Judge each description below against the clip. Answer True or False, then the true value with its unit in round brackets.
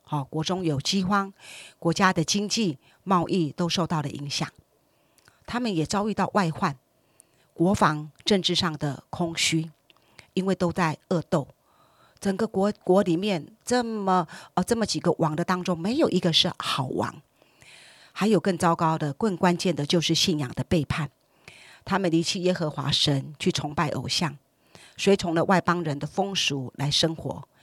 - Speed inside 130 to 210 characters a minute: False (230 characters per minute)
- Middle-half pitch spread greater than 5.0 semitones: False (3.9 semitones)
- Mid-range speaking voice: True (170 Hz)